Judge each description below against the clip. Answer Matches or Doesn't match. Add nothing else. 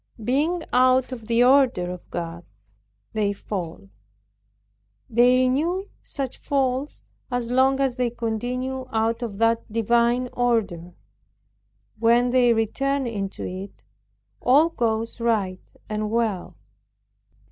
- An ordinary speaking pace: Doesn't match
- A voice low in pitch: Doesn't match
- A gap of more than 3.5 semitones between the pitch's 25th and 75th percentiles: Doesn't match